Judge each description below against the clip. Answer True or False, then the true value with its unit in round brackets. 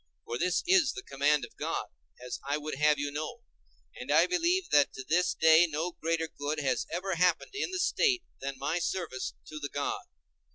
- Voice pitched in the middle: True (160 Hz)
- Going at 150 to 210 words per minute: True (200 wpm)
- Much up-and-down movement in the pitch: False (4.6 semitones)